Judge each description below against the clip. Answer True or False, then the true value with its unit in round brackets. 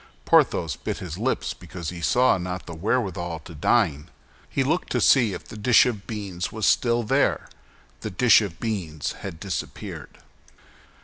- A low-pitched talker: True (100 Hz)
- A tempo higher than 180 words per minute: False (165 wpm)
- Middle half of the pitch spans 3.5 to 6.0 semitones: True (5.4 semitones)